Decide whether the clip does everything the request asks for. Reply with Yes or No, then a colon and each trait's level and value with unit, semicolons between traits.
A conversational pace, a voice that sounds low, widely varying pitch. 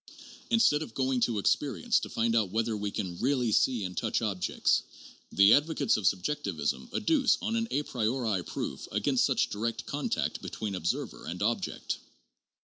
Yes: average, 160 wpm; low, 115 Hz; wide, 6.0 semitones